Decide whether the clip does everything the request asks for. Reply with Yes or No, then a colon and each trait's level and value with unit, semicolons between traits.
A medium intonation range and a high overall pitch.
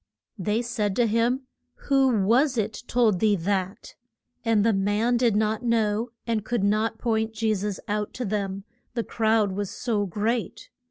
No: narrow, 2.2 semitones; high, 220 Hz